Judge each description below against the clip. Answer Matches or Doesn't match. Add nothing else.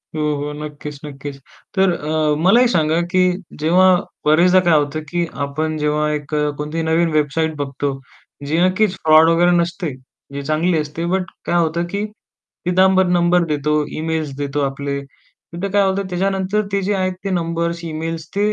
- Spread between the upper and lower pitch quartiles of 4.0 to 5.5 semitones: Doesn't match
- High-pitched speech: Doesn't match